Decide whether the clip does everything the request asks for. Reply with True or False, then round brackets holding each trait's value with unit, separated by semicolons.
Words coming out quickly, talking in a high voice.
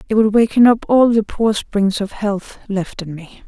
True (225 wpm; 210 Hz)